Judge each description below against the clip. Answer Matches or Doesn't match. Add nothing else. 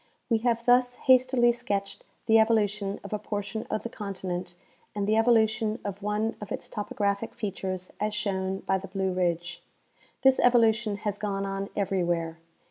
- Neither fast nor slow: Matches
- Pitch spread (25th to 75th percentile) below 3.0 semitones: Matches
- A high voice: Matches